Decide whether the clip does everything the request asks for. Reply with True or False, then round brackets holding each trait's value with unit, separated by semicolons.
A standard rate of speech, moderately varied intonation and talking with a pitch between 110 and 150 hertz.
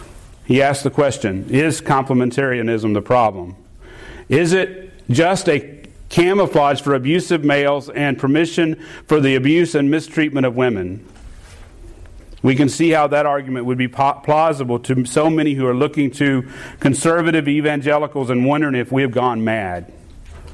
True (150 wpm; 4.1 semitones; 135 Hz)